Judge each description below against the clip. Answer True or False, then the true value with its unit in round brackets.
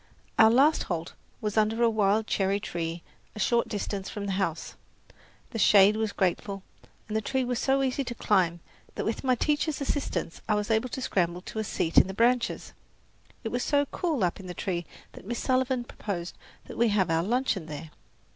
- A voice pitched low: False (215 Hz)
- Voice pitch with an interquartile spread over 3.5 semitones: True (4.5 semitones)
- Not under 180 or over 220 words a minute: True (200 wpm)